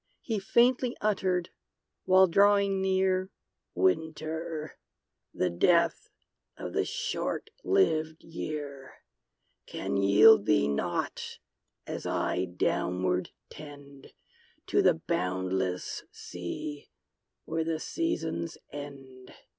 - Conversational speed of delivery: No, slow, 90 wpm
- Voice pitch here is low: No, medium, 155 Hz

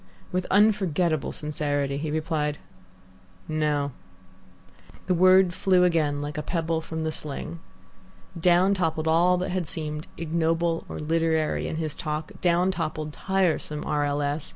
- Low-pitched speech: No, medium, 160 Hz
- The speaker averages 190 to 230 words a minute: No, average, 140 wpm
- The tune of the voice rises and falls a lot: No, narrow, 2.6 semitones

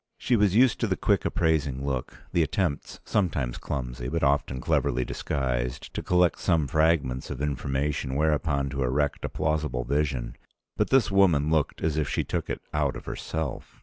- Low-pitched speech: Yes, very low, 75 Hz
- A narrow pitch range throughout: No, average, 3.2 semitones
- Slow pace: No, average, 175 wpm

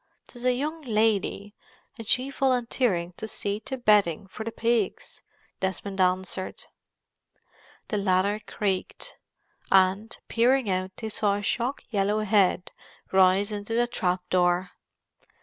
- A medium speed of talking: No, slow, 130 wpm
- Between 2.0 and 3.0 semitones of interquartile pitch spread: No, average, 3.6 semitones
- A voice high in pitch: Yes, high, 205 Hz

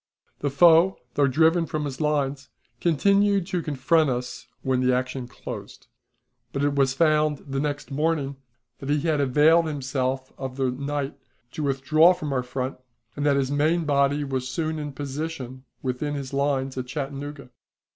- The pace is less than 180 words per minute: Yes, average, 165 wpm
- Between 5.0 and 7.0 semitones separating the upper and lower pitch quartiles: No, narrow, 2.6 semitones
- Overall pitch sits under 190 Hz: Yes, medium, 140 Hz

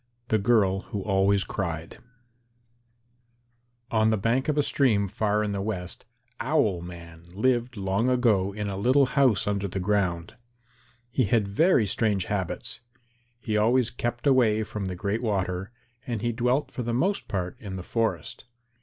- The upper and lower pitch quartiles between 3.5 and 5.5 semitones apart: Yes, average, 3.8 semitones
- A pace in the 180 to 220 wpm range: No, average, 160 wpm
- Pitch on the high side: No, low, 105 Hz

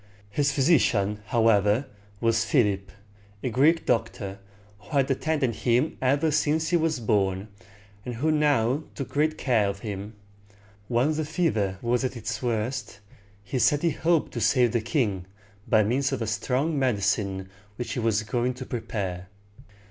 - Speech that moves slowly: No, average, 155 wpm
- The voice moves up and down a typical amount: Yes, average, 5.0 semitones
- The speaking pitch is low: Yes, low, 120 Hz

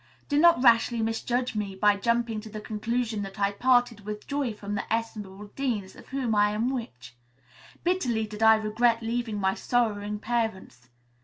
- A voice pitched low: No, high, 220 Hz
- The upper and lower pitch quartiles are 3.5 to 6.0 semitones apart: No, narrow, 2.6 semitones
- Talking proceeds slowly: No, average, 170 wpm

